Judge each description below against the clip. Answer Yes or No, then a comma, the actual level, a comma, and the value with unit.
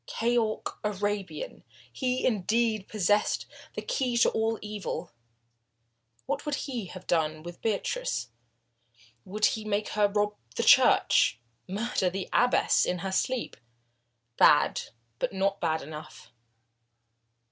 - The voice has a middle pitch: No, high, 210 Hz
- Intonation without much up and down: No, average, 3.5 semitones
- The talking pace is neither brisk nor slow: No, slow, 120 wpm